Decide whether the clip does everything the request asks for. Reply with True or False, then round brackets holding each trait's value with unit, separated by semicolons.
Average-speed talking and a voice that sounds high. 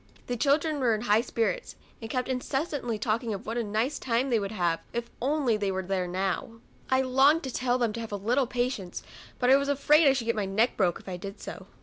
False (245 wpm; 235 Hz)